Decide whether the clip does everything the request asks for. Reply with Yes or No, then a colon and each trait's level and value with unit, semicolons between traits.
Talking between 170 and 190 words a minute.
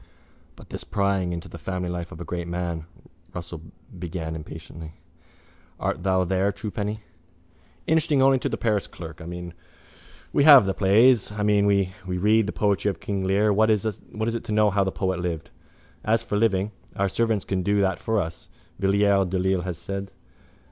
Yes: average, 185 wpm